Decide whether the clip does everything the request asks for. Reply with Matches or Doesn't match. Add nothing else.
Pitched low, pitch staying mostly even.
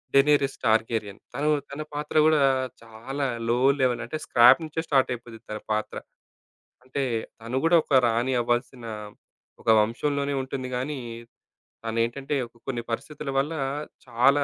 Doesn't match